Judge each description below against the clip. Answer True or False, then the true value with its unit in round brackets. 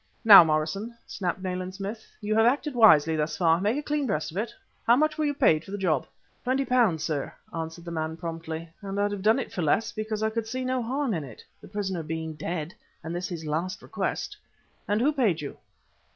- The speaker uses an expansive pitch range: True (5.9 semitones)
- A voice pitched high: True (195 Hz)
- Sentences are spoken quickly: True (225 wpm)